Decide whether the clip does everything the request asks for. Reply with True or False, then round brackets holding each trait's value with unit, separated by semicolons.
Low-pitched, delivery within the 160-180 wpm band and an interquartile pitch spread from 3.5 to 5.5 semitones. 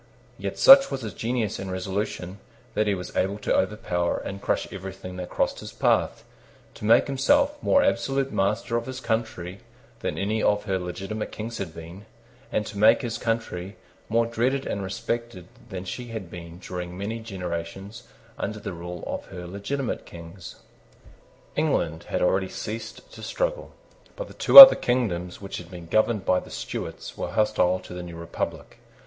True (100 Hz; 175 wpm; 4.2 semitones)